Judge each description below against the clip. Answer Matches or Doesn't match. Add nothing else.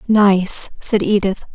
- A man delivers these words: Doesn't match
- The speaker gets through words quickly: Doesn't match